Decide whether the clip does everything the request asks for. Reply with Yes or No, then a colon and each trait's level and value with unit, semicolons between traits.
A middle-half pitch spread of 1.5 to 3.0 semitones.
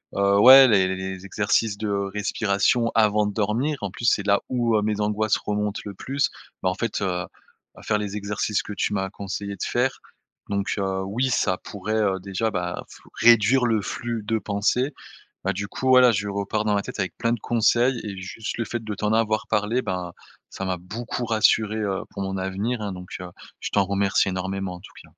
Yes: narrow, 2.4 semitones